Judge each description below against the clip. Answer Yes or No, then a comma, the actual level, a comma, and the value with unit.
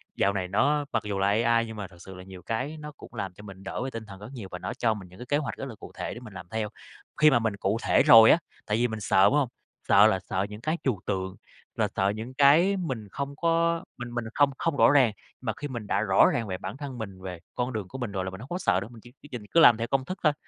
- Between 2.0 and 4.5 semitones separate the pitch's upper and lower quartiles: No, wide, 5.5 semitones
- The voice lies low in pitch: Yes, low, 115 Hz